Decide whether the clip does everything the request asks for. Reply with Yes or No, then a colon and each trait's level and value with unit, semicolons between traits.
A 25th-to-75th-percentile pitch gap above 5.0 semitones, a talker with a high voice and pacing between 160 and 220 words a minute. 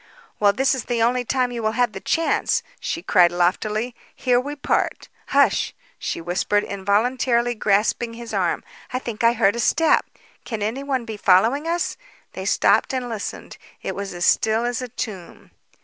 No: average, 3.4 semitones; high, 235 Hz; average, 175 wpm